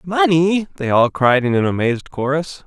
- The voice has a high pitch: No, medium, 150 Hz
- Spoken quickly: No, average, 180 wpm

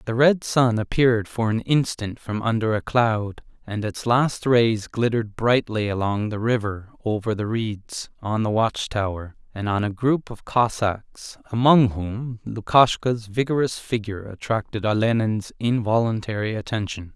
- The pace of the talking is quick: No, average, 145 wpm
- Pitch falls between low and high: No, low, 110 Hz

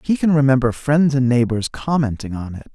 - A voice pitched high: No, low, 130 Hz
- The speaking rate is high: No, average, 195 wpm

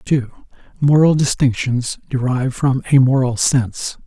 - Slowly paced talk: Yes, slow, 120 wpm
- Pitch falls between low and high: No, low, 130 Hz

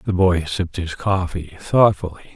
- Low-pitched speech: Yes, very low, 90 Hz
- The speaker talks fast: No, average, 155 wpm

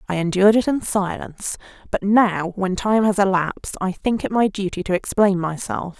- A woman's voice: Yes, female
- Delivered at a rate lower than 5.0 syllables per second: No, 5.2 syllables/s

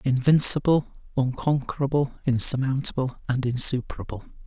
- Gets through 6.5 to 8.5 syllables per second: No, 5.2 syllables/s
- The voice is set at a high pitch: No, low, 135 Hz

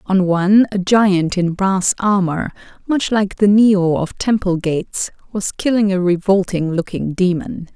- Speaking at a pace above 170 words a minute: No, average, 155 wpm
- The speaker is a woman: Yes, female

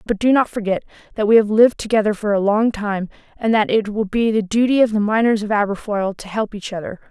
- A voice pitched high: Yes, high, 215 Hz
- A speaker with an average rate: No, fast, 245 wpm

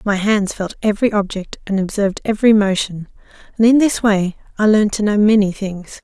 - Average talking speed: Yes, average, 190 wpm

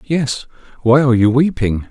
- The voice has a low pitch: Yes, low, 130 Hz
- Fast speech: No, average, 155 wpm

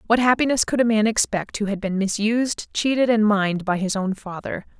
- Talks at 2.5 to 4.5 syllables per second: No, 5.6 syllables/s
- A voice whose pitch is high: Yes, high, 215 Hz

